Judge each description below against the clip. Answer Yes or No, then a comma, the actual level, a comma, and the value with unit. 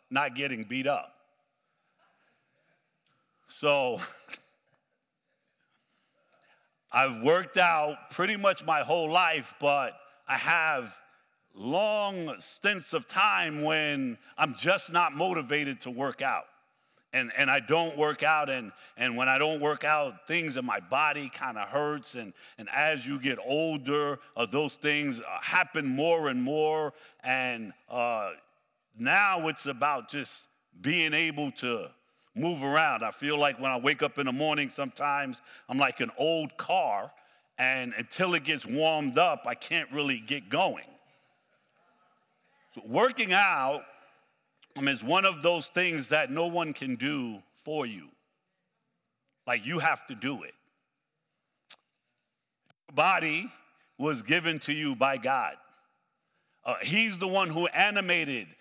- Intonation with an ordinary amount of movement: Yes, average, 3.4 semitones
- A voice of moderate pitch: Yes, medium, 150 Hz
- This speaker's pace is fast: No, average, 140 wpm